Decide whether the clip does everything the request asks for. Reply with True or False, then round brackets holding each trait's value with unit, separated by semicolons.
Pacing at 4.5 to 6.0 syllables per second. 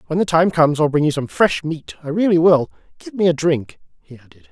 True (5.9 syllables/s)